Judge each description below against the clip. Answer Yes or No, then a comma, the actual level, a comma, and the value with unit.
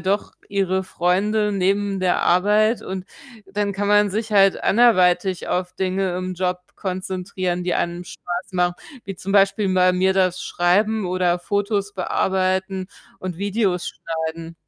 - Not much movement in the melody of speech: Yes, narrow, 1.8 semitones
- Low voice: No, high, 190 Hz